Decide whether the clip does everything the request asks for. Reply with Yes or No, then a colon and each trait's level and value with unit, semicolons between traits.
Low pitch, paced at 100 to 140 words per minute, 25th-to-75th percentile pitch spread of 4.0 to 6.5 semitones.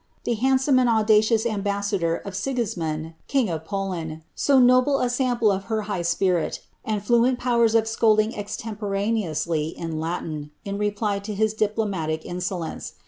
No: high, 210 Hz; slow, 135 wpm; average, 4.5 semitones